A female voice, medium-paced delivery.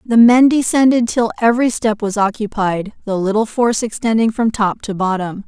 Yes: female; average, 175 wpm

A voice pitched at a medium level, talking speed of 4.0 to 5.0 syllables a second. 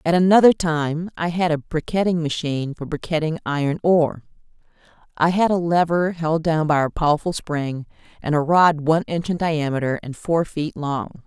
No: medium, 160 Hz; 5.2 syllables/s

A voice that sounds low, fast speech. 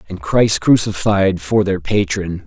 No: very low, 95 Hz; average, 145 wpm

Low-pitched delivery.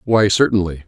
Yes: low, 100 Hz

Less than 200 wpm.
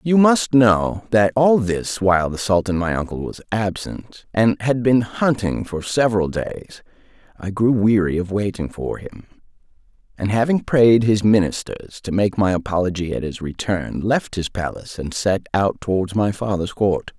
Yes: average, 170 wpm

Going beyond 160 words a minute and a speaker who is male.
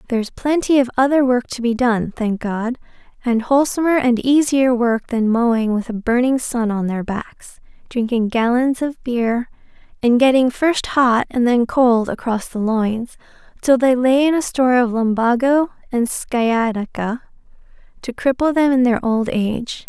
No: average, 170 wpm; female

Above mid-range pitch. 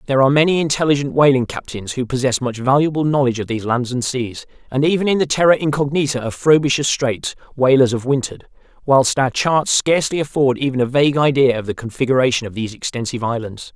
No: low, 135 Hz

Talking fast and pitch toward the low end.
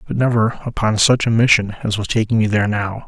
Yes: fast, 235 wpm; low, 110 Hz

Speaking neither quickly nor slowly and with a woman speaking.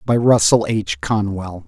No: average, 145 wpm; male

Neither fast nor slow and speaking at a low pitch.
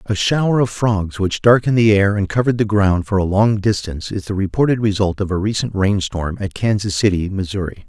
No: fast, 215 wpm; low, 100 Hz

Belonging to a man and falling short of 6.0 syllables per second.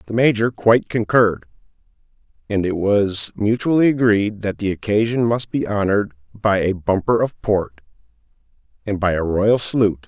Yes: male; 5.1 syllables/s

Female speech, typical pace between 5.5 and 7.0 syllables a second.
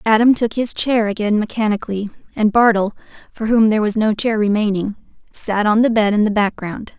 Yes: female; 5.6 syllables/s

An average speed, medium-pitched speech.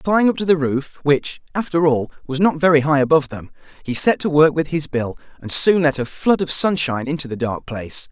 No: fast, 230 wpm; medium, 150 Hz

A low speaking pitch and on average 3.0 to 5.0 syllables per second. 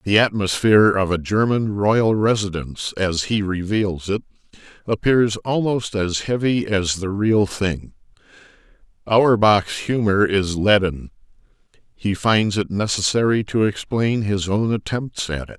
Yes: low, 100 Hz; 4.2 syllables/s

